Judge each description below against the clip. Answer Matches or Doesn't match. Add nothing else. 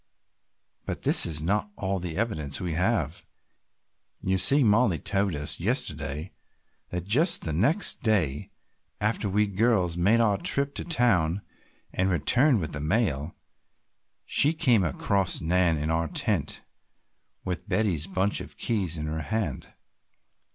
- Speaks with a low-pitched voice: Matches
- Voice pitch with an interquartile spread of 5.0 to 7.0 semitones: Matches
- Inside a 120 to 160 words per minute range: Matches